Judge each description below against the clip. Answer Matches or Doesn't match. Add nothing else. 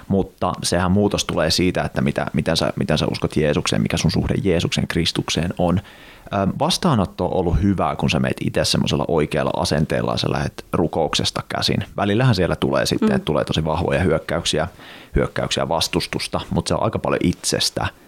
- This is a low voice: Matches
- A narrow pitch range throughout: Doesn't match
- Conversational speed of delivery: Doesn't match